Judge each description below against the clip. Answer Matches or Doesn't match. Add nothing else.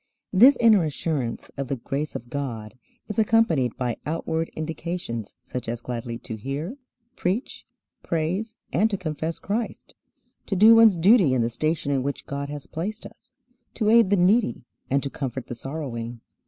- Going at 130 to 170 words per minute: Matches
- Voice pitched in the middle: Matches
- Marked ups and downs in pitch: Matches